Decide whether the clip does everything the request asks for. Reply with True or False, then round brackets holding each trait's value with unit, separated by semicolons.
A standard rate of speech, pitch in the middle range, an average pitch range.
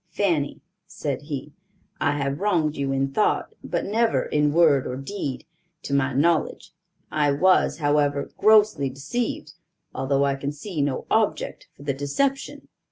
True (150 wpm; 145 Hz; 3.7 semitones)